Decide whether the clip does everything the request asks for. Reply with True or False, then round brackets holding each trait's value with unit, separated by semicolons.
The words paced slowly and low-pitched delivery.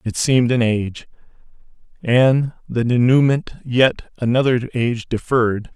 True (115 wpm; 125 Hz)